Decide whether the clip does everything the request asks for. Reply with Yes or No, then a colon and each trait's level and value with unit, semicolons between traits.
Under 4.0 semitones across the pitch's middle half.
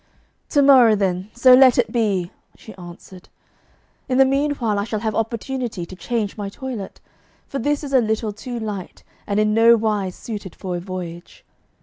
No: average, 4.4 semitones